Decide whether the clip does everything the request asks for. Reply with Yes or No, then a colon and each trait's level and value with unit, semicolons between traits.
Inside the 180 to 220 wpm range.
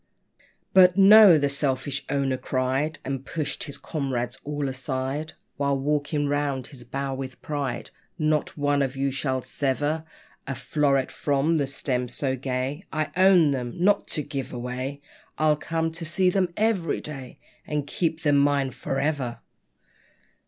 No: average, 150 wpm